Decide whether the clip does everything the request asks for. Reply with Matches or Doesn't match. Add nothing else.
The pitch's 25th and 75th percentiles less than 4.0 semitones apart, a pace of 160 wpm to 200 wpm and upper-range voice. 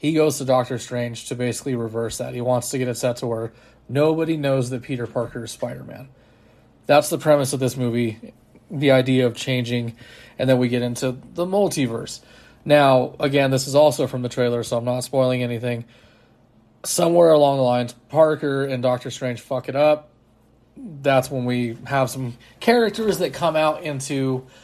Doesn't match